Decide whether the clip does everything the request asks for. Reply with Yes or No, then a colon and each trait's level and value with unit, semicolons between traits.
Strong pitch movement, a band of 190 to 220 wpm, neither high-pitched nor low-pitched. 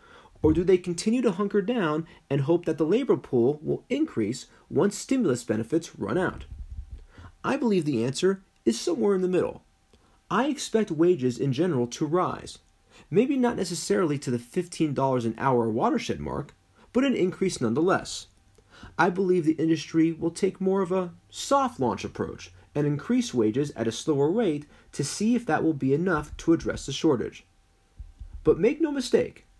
No: wide, 8.6 semitones; average, 170 wpm; medium, 160 Hz